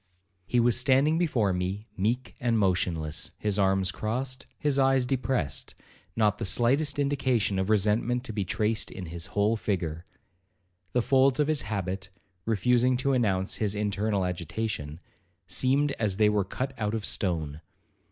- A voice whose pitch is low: Yes, low, 110 Hz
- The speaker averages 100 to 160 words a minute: Yes, average, 150 wpm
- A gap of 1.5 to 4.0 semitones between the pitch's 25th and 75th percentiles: No, average, 5.0 semitones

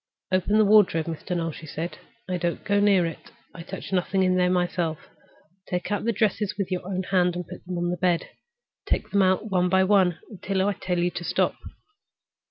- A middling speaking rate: No, fast, 210 wpm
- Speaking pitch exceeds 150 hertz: Yes, medium, 185 Hz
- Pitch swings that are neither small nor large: No, narrow, 1.9 semitones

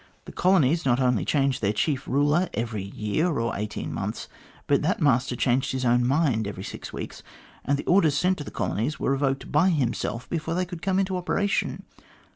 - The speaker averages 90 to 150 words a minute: No, average, 195 wpm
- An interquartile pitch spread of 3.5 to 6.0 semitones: Yes, wide, 5.5 semitones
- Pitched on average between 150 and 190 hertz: No, medium, 140 Hz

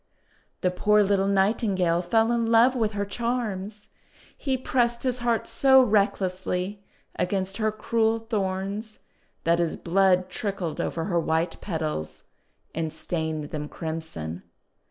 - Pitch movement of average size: Yes, average, 4.6 semitones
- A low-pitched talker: No, high, 195 Hz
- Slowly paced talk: Yes, slow, 130 wpm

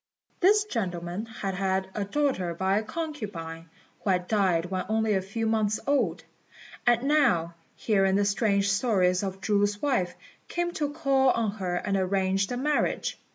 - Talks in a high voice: Yes, high, 200 Hz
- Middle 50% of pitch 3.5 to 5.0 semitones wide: Yes, average, 4.3 semitones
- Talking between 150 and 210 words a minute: Yes, average, 160 wpm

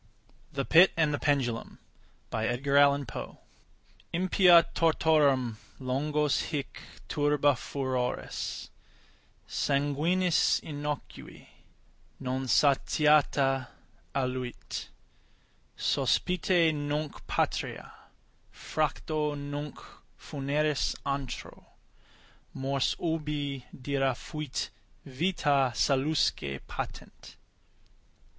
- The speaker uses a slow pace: Yes, slow, 65 wpm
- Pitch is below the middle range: No, medium, 145 Hz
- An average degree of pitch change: No, narrow, 2.3 semitones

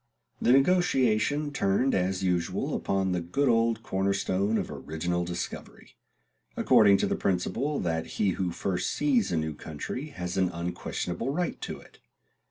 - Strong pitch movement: Yes, wide, 6.3 semitones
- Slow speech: No, average, 155 wpm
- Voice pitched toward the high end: No, very low, 95 Hz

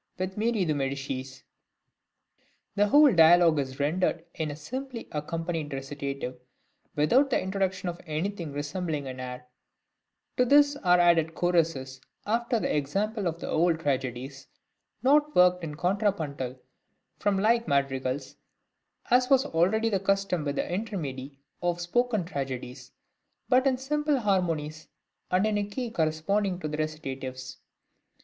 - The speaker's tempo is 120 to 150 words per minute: Yes, average, 140 wpm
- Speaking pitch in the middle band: Yes, medium, 170 Hz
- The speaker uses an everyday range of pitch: No, wide, 6.3 semitones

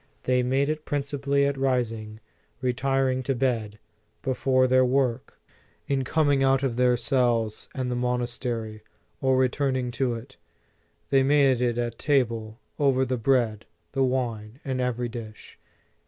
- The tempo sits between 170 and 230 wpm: No, average, 140 wpm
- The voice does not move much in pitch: Yes, narrow, 2.1 semitones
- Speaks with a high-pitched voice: No, low, 130 Hz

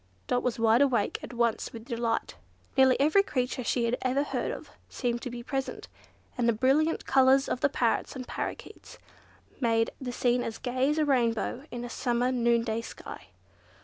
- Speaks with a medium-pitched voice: No, high, 245 Hz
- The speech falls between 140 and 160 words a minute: No, average, 180 wpm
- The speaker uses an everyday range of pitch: No, narrow, 2.1 semitones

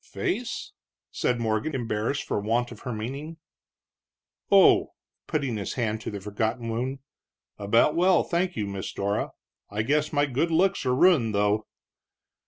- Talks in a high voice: No, low, 120 Hz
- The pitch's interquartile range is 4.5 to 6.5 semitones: Yes, average, 5.3 semitones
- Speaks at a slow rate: No, average, 150 wpm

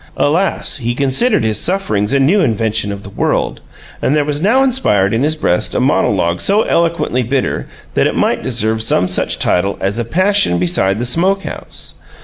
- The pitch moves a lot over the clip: Yes, wide, 8.8 semitones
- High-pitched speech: No, low, 125 Hz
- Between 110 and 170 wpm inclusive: No, average, 185 wpm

